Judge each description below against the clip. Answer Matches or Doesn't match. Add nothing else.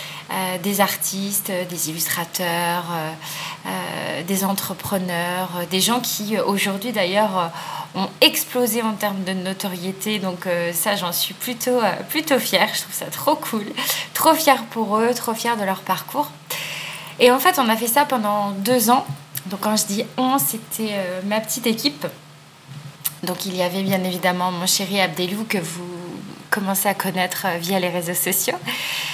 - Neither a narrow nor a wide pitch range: Matches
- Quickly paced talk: Doesn't match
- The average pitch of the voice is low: Doesn't match